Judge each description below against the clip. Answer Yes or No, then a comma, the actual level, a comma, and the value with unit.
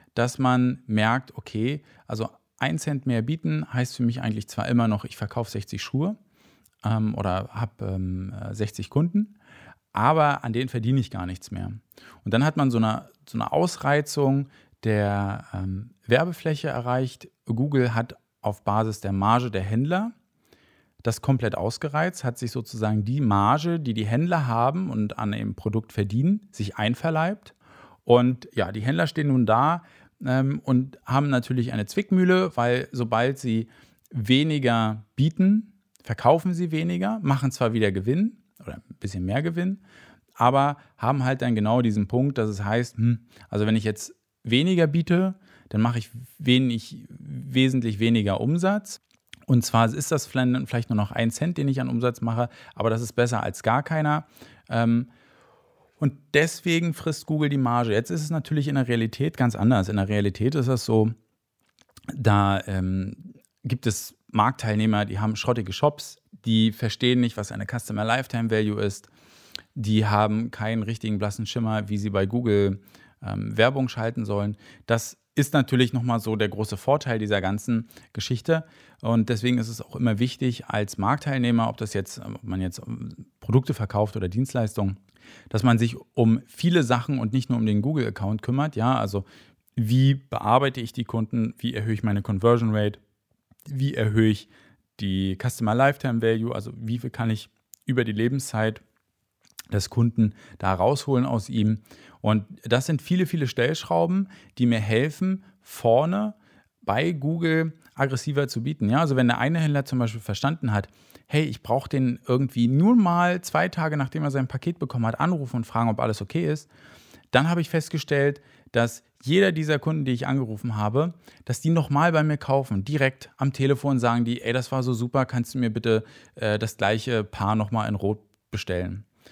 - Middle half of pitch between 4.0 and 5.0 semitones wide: Yes, average, 4.3 semitones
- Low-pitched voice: Yes, low, 120 Hz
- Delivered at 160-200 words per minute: Yes, average, 170 wpm